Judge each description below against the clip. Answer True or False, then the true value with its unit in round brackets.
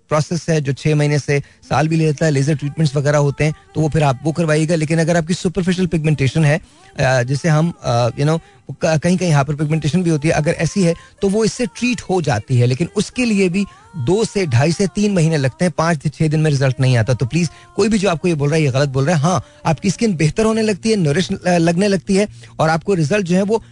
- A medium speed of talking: False (255 wpm)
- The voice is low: False (160 Hz)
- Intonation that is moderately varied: True (3.9 semitones)